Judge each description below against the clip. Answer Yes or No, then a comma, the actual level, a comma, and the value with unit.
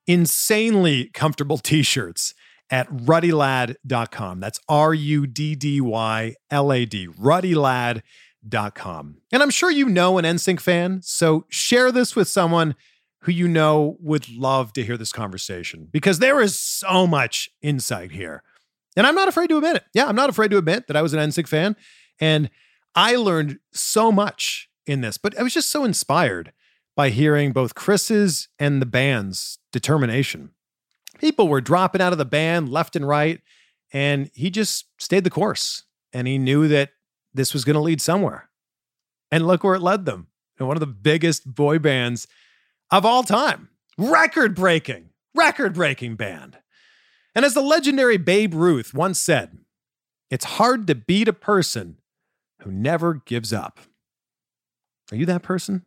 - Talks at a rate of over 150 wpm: Yes, average, 165 wpm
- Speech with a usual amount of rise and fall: No, wide, 6.4 semitones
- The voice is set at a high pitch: No, medium, 155 Hz